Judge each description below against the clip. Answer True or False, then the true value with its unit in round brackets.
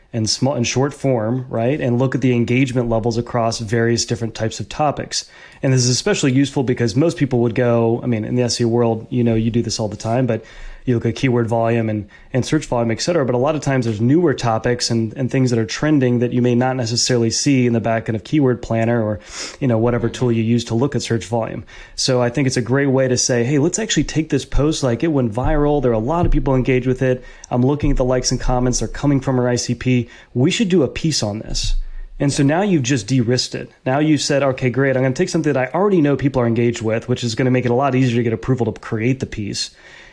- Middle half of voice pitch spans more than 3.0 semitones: False (2.7 semitones)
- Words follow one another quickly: True (270 wpm)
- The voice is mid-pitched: False (125 Hz)